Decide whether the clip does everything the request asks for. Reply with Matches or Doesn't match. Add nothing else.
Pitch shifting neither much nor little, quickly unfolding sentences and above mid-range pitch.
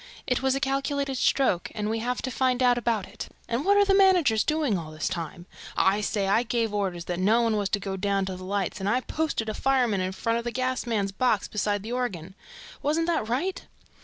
Matches